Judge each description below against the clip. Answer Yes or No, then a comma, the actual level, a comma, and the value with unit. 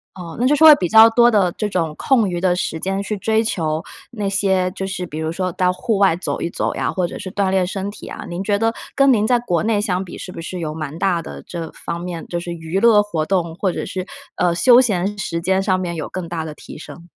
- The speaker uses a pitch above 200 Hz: No, medium, 185 Hz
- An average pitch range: Yes, average, 3.3 semitones